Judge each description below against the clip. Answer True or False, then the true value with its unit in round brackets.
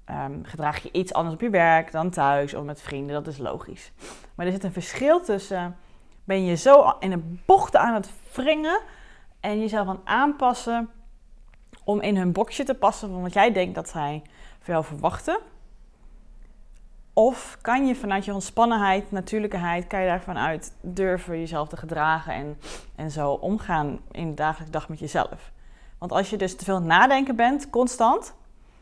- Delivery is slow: False (175 wpm)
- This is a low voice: False (185 Hz)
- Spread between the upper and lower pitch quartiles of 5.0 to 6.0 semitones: True (5.4 semitones)